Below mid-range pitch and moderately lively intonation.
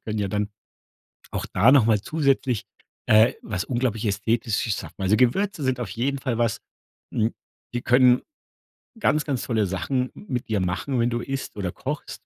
Yes: low, 120 Hz; average, 3.7 semitones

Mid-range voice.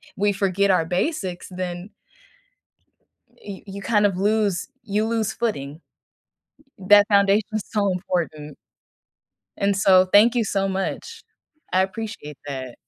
No: high, 195 Hz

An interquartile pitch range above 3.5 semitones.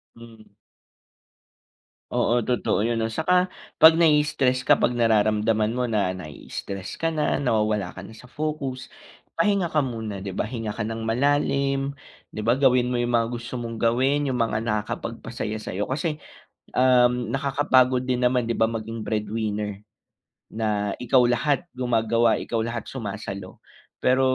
No: average, 3.2 semitones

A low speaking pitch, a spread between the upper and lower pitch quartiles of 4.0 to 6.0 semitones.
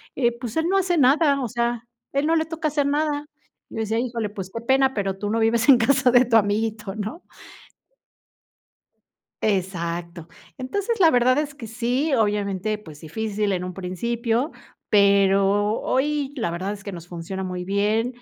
No: high, 225 Hz; average, 5.1 semitones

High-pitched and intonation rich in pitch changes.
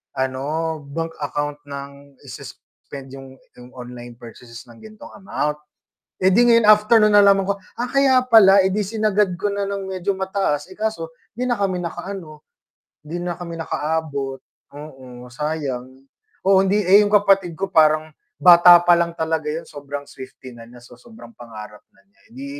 No: medium, 165 Hz; wide, 6.0 semitones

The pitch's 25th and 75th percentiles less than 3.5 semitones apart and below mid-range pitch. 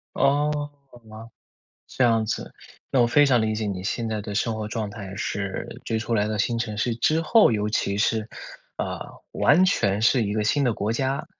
Yes: average, 2.9 semitones; low, 110 Hz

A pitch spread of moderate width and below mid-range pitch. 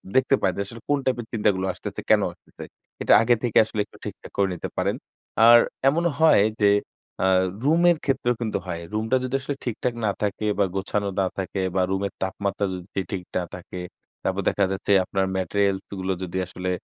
Yes: average, 4.1 semitones; low, 100 Hz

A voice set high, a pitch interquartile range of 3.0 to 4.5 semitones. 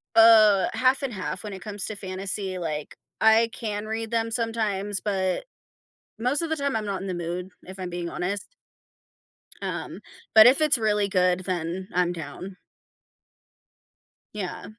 Yes: high, 200 Hz; average, 3.4 semitones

